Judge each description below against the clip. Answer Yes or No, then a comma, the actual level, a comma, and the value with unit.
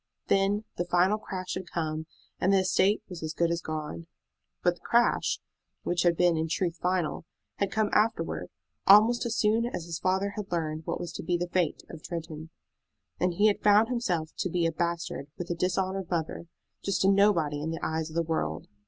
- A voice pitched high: No, medium, 175 Hz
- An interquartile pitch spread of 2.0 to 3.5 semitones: Yes, average, 3.2 semitones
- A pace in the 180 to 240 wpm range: Yes, fast, 205 wpm